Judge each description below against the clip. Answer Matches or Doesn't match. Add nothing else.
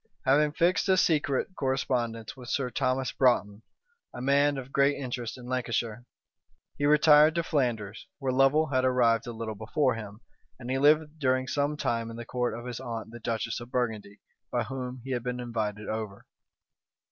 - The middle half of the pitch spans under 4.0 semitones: Matches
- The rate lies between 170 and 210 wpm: Matches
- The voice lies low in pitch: Matches